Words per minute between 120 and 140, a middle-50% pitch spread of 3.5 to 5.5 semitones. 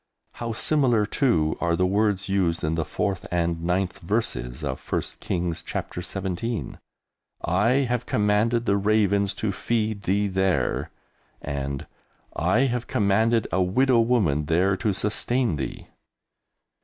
Yes: slow, 135 wpm; average, 4.6 semitones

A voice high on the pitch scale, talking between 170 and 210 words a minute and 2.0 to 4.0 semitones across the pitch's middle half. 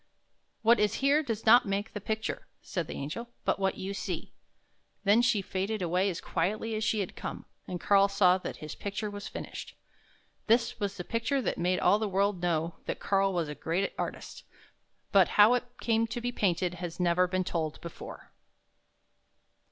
Yes: high, 200 Hz; average, 190 wpm; average, 3.4 semitones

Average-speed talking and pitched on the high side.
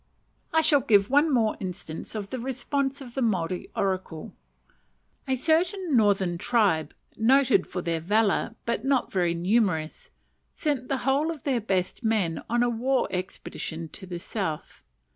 Yes: average, 155 wpm; high, 220 Hz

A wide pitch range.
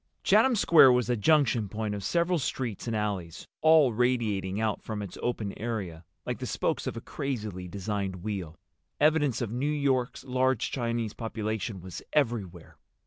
No: average, 4.4 semitones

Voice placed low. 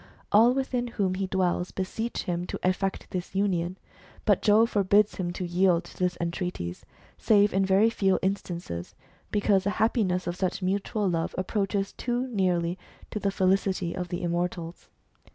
No: high, 190 Hz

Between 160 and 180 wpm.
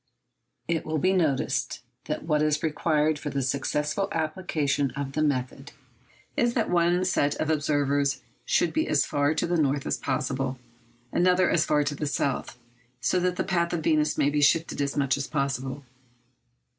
Yes: average, 175 wpm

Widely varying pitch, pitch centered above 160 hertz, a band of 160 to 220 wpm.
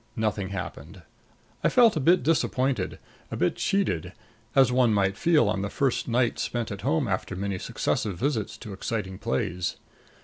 No: wide, 5.8 semitones; low, 110 Hz; average, 165 wpm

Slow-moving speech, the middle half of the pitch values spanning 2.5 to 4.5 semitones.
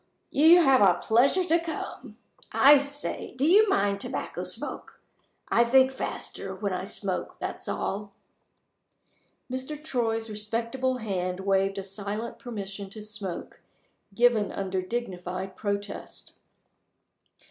No: slow, 125 wpm; average, 4.9 semitones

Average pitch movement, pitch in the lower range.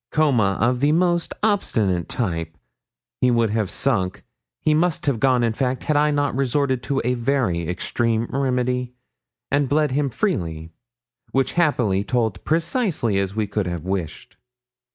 No: wide, 5.9 semitones; low, 125 Hz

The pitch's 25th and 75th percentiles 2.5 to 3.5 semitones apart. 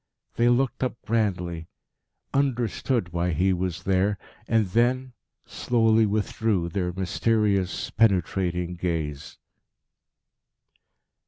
No: average, 4.3 semitones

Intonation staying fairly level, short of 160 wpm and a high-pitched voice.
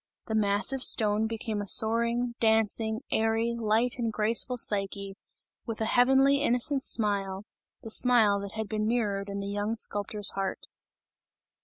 Yes: narrow, 2.3 semitones; average, 145 wpm; high, 220 Hz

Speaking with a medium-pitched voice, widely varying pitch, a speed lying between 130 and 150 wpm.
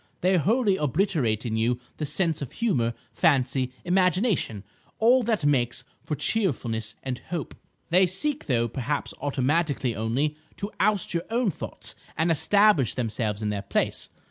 Yes: medium, 150 Hz; wide, 8.0 semitones; average, 145 wpm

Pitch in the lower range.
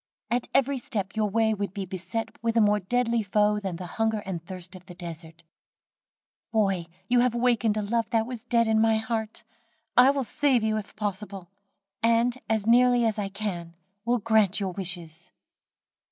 No: high, 215 Hz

